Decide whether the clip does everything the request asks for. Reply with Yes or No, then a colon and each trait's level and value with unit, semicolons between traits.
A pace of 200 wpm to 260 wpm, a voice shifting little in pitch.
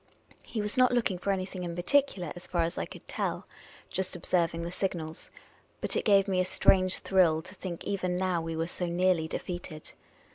Yes: fast, 205 wpm; narrow, 2.0 semitones